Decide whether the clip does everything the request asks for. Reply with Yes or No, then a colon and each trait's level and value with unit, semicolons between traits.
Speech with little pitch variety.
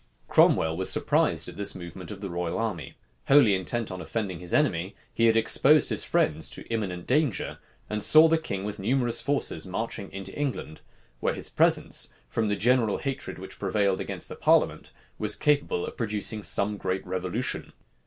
No: average, 4.2 semitones